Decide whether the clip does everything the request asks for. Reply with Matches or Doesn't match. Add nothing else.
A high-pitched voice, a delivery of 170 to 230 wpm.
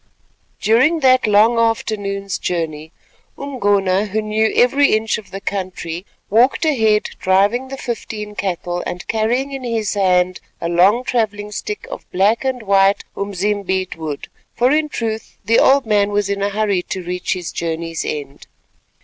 Doesn't match